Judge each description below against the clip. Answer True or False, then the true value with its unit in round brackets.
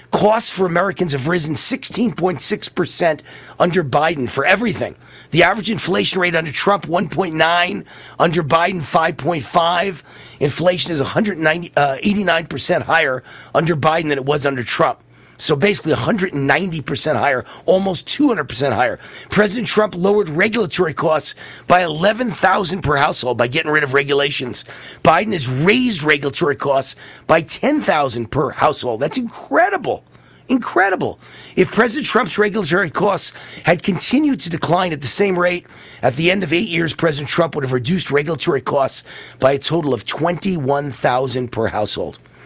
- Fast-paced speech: False (140 wpm)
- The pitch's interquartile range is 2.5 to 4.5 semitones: False (5.2 semitones)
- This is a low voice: False (170 Hz)